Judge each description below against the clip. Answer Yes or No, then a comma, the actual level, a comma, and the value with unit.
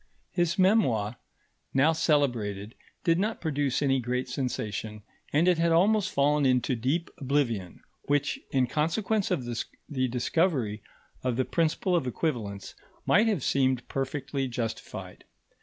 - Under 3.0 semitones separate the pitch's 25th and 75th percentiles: No, average, 5.1 semitones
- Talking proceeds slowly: Yes, slow, 130 wpm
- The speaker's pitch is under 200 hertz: Yes, low, 135 Hz